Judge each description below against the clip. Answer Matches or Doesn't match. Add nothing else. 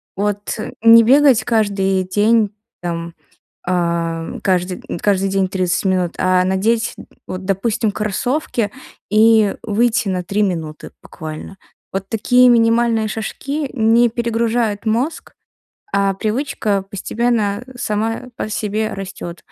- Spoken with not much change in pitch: Doesn't match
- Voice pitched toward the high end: Matches